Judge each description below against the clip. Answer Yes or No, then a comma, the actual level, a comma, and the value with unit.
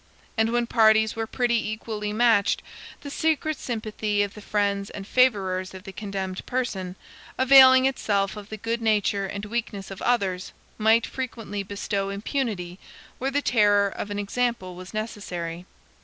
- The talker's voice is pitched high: Yes, high, 210 Hz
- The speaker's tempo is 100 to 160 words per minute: Yes, average, 155 wpm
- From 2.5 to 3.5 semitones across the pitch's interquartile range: Yes, average, 3.0 semitones